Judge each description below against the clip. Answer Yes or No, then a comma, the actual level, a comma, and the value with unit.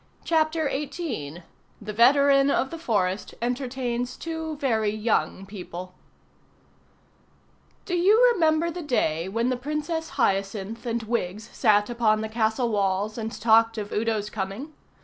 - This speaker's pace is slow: Yes, slow, 130 wpm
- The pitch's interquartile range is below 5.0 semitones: No, wide, 5.4 semitones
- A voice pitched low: No, high, 235 Hz